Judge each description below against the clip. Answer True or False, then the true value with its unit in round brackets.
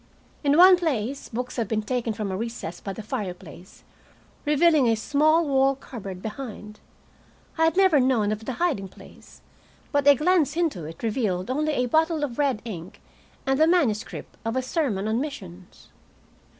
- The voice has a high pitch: True (250 Hz)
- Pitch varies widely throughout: True (5.9 semitones)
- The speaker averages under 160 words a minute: False (170 wpm)